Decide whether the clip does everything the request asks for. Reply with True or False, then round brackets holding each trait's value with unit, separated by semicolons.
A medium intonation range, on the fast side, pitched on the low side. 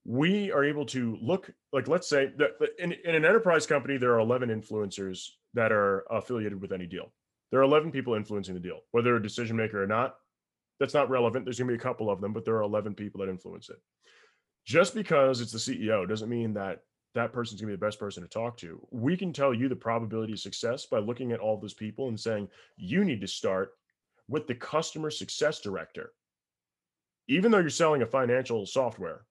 True (4.8 semitones; 220 wpm; 120 Hz)